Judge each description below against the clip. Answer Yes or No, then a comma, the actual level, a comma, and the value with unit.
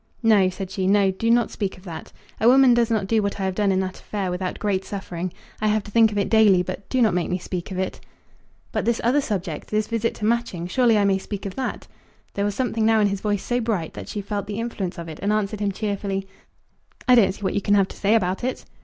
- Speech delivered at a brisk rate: Yes, fast, 270 wpm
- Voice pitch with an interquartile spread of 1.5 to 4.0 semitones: Yes, average, 2.8 semitones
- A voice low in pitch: No, high, 205 Hz